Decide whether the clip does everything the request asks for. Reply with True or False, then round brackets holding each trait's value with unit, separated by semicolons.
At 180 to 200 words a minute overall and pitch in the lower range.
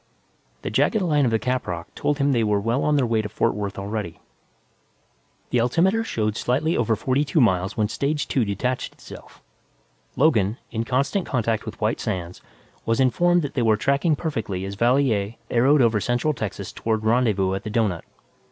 True (185 wpm; 115 Hz)